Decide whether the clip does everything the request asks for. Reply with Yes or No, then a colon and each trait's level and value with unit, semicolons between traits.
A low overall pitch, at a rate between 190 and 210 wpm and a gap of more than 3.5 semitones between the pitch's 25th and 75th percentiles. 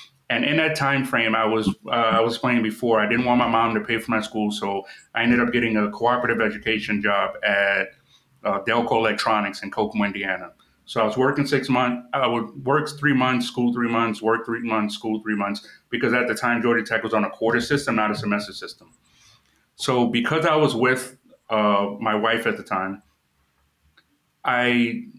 No: low, 115 Hz; average, 200 wpm; narrow, 2.6 semitones